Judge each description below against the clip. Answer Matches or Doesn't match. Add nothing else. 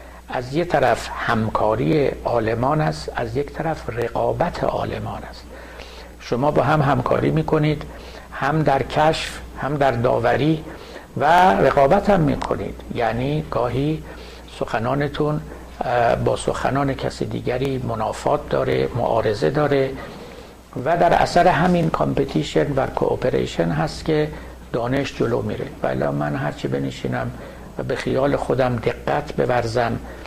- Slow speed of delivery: Doesn't match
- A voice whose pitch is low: Matches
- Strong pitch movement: Matches